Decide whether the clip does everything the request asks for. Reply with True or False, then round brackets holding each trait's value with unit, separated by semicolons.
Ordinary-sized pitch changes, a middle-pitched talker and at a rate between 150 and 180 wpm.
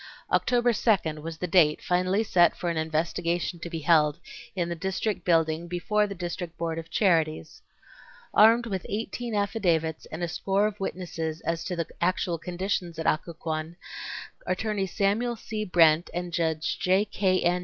True (3.2 semitones; 175 Hz; 165 wpm)